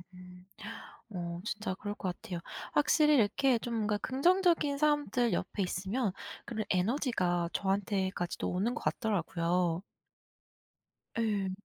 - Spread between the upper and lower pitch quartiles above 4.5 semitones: Yes, average, 5.2 semitones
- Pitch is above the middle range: Yes, high, 205 Hz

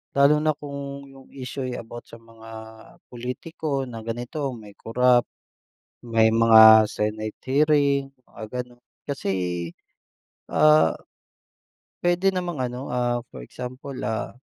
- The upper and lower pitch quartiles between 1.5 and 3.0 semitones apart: No, average, 3.6 semitones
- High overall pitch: No, low, 125 Hz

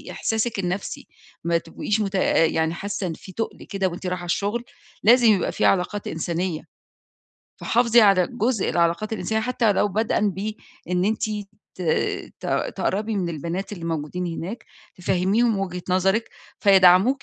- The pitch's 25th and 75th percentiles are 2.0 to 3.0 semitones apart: No, average, 3.5 semitones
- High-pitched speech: Yes, high, 195 Hz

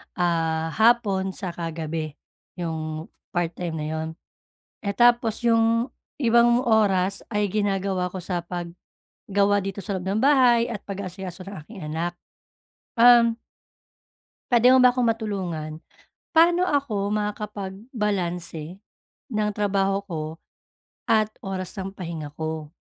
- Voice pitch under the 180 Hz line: No, high, 195 Hz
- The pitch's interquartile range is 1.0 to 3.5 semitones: No, average, 4.6 semitones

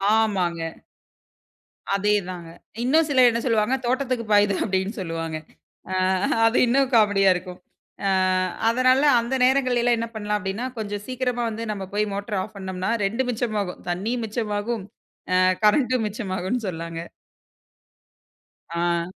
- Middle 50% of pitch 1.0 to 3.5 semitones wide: No, average, 4.3 semitones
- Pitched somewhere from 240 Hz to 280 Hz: No, high, 210 Hz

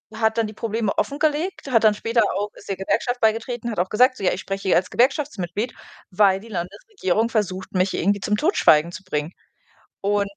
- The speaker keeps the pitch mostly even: No, average, 3.5 semitones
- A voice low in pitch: No, high, 210 Hz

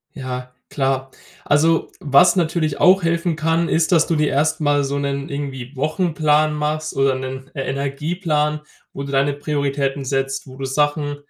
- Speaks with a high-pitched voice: No, medium, 145 Hz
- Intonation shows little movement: Yes, narrow, 2.3 semitones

